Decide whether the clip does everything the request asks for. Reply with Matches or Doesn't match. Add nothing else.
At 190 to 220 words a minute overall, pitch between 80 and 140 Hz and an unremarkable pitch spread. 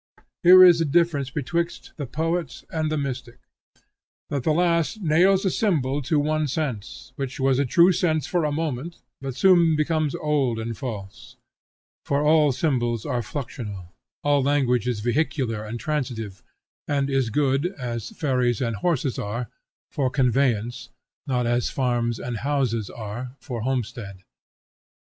Doesn't match